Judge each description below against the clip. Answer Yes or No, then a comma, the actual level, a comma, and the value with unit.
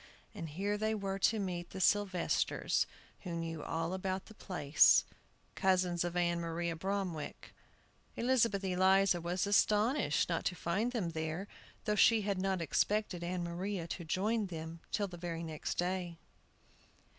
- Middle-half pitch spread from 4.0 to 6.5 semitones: No, average, 2.9 semitones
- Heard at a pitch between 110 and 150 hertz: No, medium, 185 Hz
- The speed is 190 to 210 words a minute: No, average, 150 wpm